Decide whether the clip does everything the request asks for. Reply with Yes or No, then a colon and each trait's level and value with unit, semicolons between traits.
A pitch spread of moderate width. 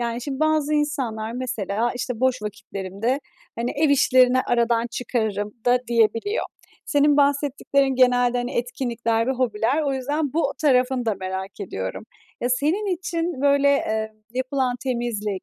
Yes: average, 3.7 semitones